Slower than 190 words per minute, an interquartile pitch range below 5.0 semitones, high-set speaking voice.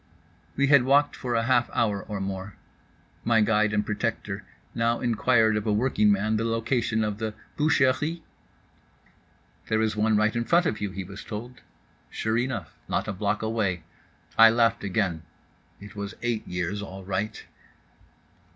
No: average, 160 wpm; narrow, 2.4 semitones; low, 110 Hz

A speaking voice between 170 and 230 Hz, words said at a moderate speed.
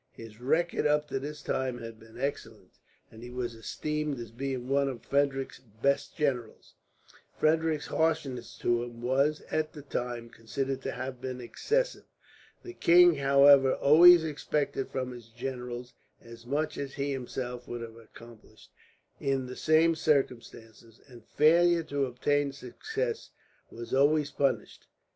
No: low, 135 Hz; average, 145 wpm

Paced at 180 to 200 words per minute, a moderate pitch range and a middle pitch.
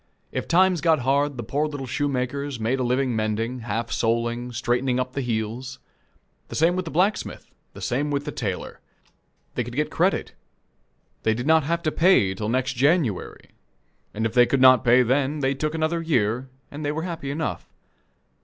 No: average, 190 wpm; average, 4.1 semitones; low, 130 Hz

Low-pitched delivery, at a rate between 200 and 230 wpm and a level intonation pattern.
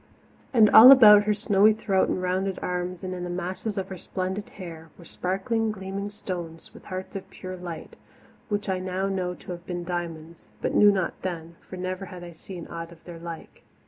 No: medium, 185 Hz; fast, 205 wpm; narrow, 2.1 semitones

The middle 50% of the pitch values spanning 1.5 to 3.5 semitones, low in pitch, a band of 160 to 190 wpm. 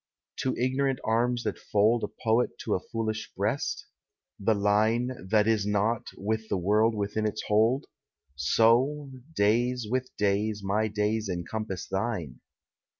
No: narrow, 2.5 semitones; low, 110 Hz; average, 140 wpm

